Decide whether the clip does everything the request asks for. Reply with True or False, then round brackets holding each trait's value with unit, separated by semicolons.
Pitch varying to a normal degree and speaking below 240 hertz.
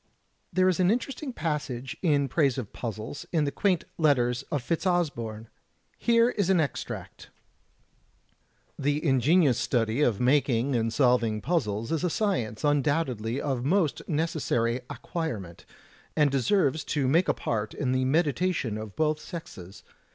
False (5.7 semitones; 140 Hz)